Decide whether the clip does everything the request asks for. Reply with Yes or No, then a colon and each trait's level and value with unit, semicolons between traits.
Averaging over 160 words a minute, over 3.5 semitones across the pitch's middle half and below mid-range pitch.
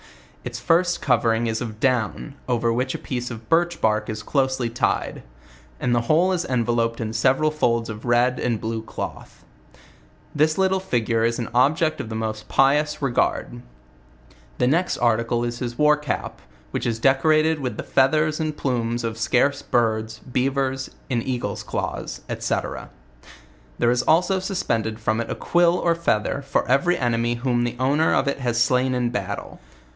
Yes: average, 170 wpm; average, 4.2 semitones; low, 125 Hz